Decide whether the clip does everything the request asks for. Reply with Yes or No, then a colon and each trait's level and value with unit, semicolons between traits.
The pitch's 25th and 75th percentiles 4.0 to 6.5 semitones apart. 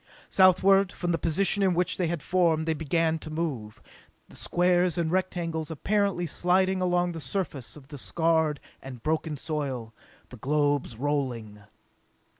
No: average, 3.6 semitones